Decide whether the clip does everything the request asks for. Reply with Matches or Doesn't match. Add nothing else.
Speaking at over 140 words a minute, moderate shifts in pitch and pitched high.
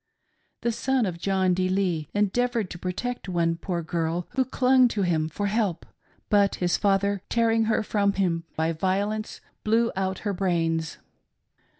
Matches